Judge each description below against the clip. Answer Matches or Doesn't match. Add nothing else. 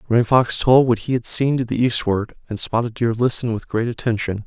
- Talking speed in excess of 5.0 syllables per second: Matches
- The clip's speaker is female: Doesn't match